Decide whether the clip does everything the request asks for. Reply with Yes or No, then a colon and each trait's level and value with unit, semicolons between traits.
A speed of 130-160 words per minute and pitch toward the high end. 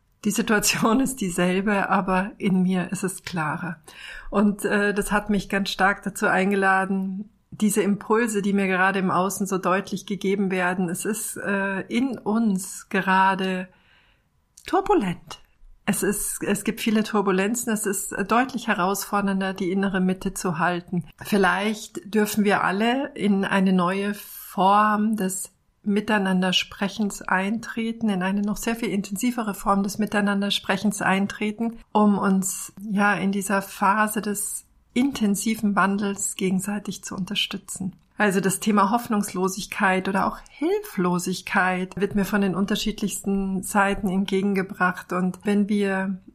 Yes: average, 135 wpm; high, 200 Hz